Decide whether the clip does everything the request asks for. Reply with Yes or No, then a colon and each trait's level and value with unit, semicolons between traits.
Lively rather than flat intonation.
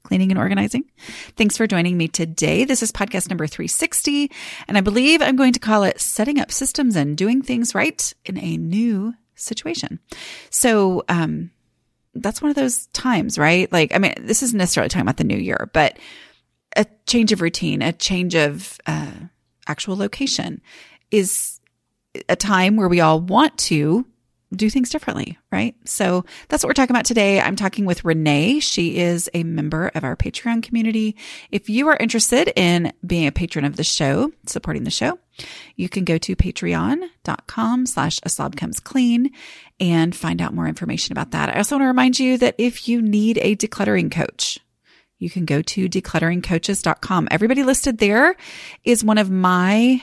Yes: wide, 6.5 semitones